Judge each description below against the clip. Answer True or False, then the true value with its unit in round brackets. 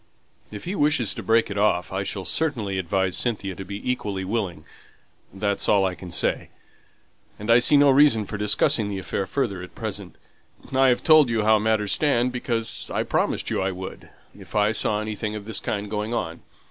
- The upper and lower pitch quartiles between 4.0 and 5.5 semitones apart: False (3.3 semitones)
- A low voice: True (105 Hz)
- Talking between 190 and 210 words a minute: True (195 wpm)